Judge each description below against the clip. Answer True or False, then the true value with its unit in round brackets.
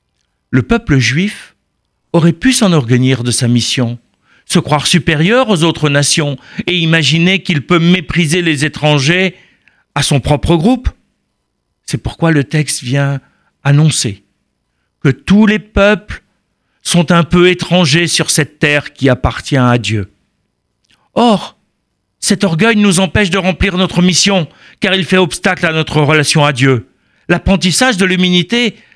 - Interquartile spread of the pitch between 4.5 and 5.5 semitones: True (4.8 semitones)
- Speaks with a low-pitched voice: False (165 Hz)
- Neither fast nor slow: False (140 wpm)